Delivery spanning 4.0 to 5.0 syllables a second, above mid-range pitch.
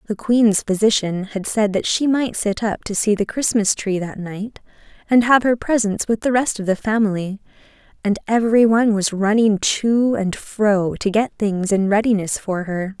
Yes: 4.7 syllables/s; high, 210 Hz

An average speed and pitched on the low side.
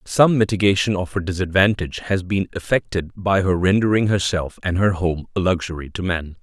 Yes: average, 175 wpm; very low, 95 Hz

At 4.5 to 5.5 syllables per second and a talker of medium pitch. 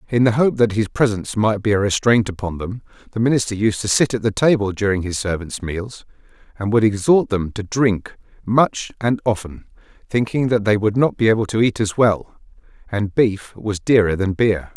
No: 5.1 syllables/s; low, 110 Hz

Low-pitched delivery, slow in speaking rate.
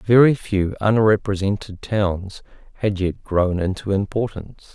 Yes: low, 100 Hz; slow, 115 wpm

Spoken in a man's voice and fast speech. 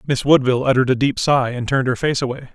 Yes: male; fast, 260 wpm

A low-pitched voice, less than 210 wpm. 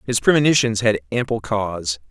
Yes: low, 110 Hz; average, 140 wpm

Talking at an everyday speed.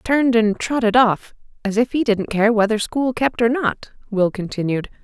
Yes: average, 190 wpm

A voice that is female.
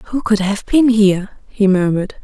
Yes: female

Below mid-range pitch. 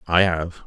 Yes: very low, 85 Hz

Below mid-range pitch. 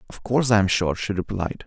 Yes: low, 100 Hz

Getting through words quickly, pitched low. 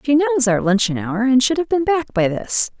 No: fast, 255 wpm; very high, 250 Hz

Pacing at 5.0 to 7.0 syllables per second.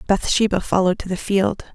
Yes: 6.0 syllables/s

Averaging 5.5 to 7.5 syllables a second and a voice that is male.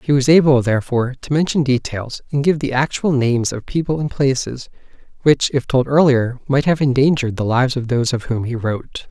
Yes: 5.8 syllables/s; male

